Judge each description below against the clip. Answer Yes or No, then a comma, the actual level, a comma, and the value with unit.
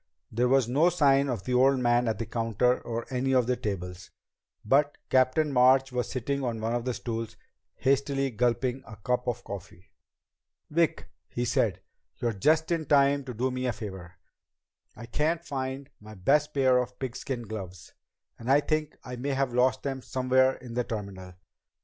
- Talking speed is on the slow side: No, average, 180 wpm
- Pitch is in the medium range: No, low, 125 Hz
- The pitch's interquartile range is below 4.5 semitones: Yes, average, 2.9 semitones